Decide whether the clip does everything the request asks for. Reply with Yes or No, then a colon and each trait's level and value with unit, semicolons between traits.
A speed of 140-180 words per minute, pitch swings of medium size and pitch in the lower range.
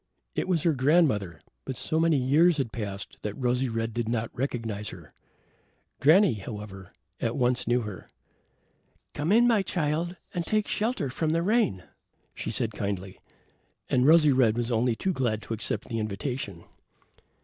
No: average, 160 wpm; wide, 6.7 semitones; low, 125 Hz